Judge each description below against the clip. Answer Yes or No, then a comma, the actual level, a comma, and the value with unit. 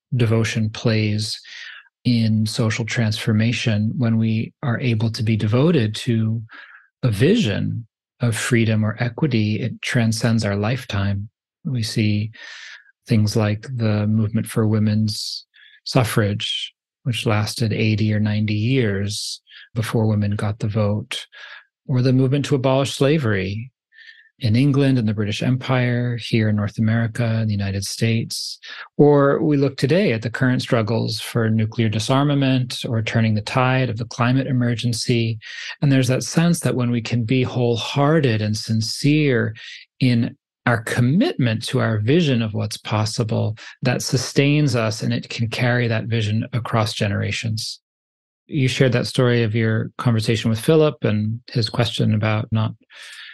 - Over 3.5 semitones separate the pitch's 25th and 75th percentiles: No, average, 2.8 semitones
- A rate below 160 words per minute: Yes, average, 145 wpm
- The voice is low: Yes, low, 115 Hz